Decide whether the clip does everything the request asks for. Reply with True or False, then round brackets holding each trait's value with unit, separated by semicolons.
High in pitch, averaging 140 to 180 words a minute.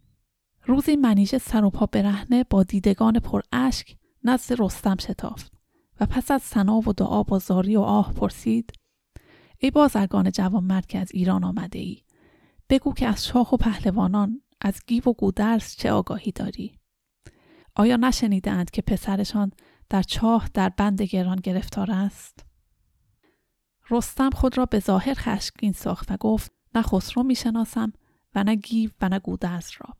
True (210 Hz; 150 wpm)